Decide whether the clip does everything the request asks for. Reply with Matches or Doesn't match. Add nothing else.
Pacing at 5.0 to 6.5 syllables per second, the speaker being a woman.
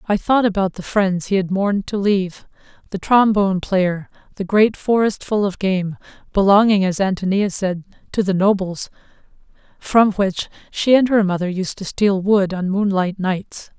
Doesn't match